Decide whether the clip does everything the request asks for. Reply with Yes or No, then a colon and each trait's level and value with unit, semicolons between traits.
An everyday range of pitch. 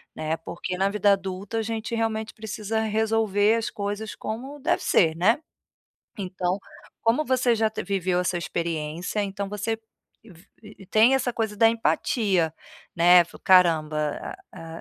Yes: average, 3.7 semitones